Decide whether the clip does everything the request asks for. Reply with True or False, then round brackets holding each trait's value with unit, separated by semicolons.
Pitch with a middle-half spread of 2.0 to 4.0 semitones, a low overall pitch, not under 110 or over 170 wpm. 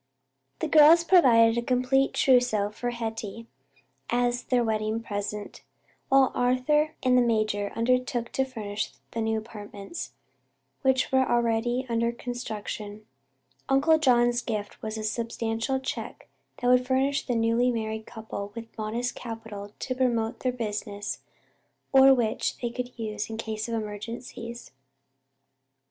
False (2.4 semitones; 235 Hz; 135 wpm)